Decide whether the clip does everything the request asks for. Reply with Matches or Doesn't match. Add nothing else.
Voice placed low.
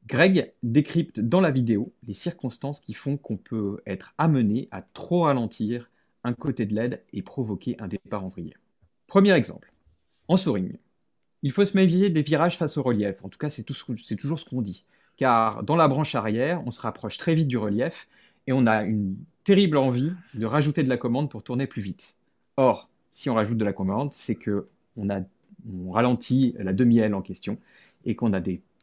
Matches